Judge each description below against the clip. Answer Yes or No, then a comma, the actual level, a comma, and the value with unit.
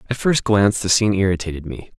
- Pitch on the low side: Yes, low, 100 Hz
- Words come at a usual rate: No, fast, 210 wpm